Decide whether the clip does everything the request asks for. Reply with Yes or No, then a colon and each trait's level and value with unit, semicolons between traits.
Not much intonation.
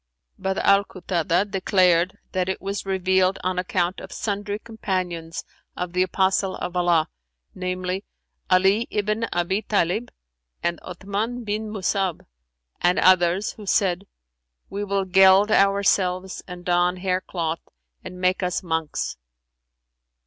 Yes: narrow, 1.8 semitones